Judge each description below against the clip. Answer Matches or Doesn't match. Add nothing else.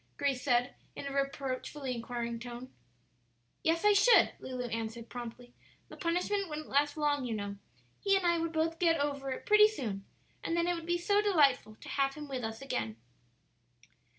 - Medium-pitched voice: Doesn't match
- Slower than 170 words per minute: Doesn't match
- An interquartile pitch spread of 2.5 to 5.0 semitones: Doesn't match